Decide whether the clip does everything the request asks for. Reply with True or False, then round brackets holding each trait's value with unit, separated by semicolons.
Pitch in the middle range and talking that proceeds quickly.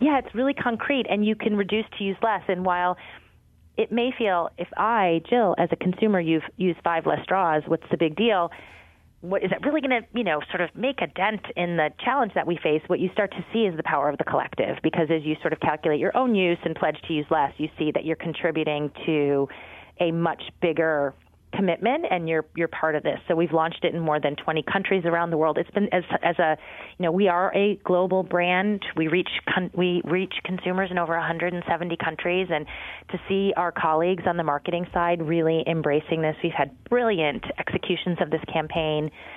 True (175 Hz; 220 wpm)